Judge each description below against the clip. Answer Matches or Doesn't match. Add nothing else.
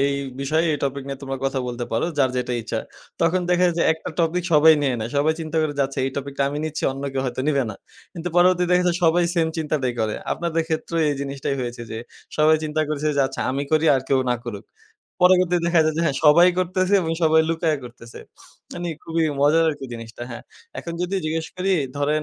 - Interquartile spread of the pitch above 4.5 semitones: Doesn't match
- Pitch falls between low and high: Matches